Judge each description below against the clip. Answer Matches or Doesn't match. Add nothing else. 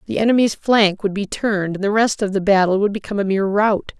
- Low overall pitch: Doesn't match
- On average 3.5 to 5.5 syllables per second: Doesn't match